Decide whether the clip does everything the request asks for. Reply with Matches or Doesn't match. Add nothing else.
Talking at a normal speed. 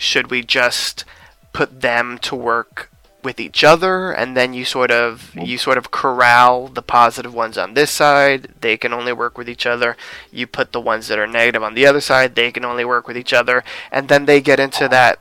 Doesn't match